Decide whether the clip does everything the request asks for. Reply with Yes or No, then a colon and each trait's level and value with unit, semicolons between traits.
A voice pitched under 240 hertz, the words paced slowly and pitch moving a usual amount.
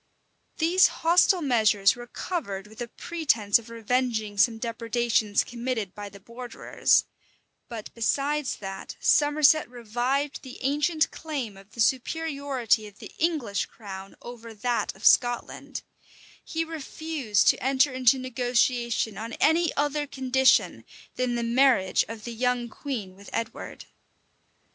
No: high, 245 Hz; slow, 130 wpm; average, 4.1 semitones